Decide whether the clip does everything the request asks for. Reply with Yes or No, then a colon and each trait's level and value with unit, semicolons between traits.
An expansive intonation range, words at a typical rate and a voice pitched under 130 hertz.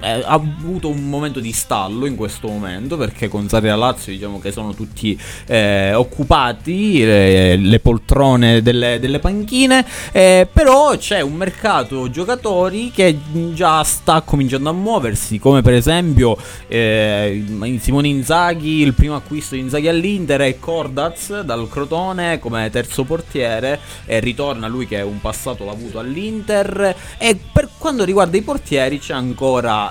No: wide, 7.1 semitones; average, 155 wpm; low, 135 Hz